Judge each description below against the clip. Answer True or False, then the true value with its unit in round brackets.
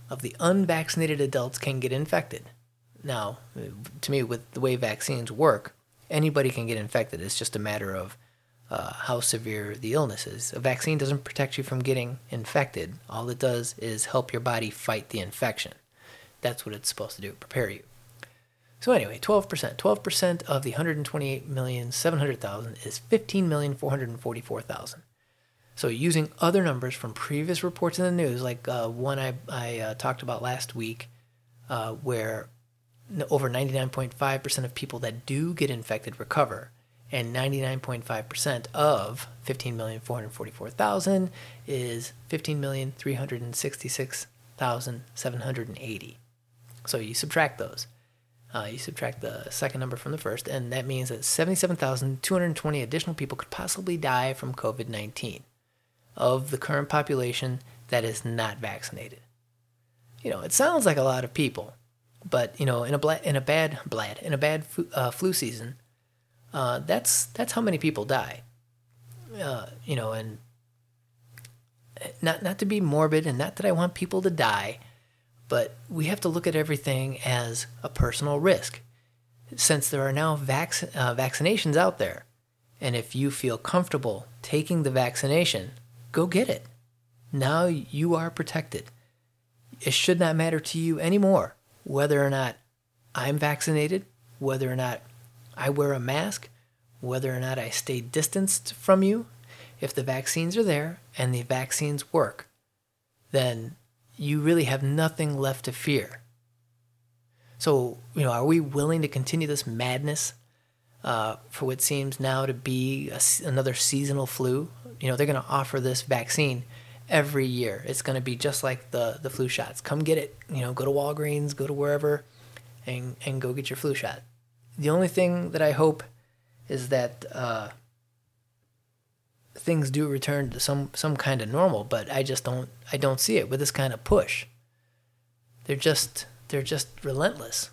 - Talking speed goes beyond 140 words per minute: True (155 wpm)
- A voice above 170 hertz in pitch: False (130 Hz)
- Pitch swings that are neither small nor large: True (3.3 semitones)